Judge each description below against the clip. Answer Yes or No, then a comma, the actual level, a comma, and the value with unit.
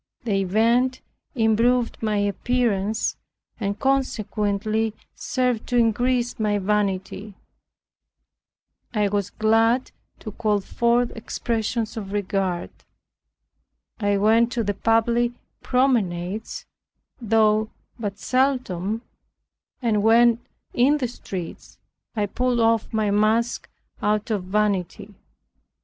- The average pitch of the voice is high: Yes, high, 220 Hz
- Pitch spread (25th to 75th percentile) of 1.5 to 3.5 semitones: Yes, narrow, 2.6 semitones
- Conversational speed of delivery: No, slow, 100 wpm